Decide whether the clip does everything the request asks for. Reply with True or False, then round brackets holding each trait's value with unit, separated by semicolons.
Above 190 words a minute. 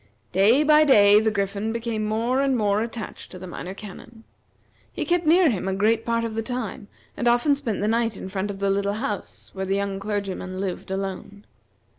True (205 wpm)